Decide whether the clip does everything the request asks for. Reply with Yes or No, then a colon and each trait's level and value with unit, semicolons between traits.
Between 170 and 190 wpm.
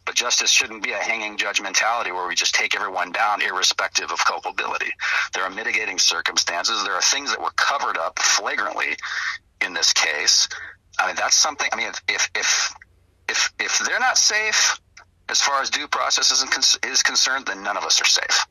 Yes: average, 185 wpm